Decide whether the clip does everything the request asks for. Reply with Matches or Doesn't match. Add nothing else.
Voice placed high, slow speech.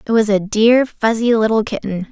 Doesn't match